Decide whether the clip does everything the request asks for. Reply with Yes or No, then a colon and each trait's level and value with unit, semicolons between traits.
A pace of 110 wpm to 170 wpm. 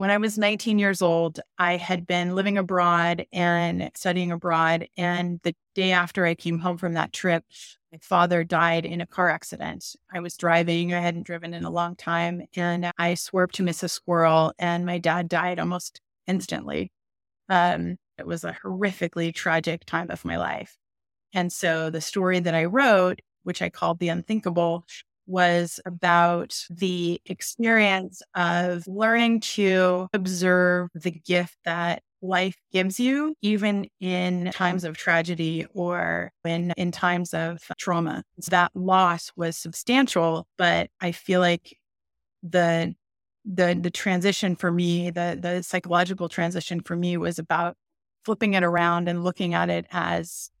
Yes: average, 155 wpm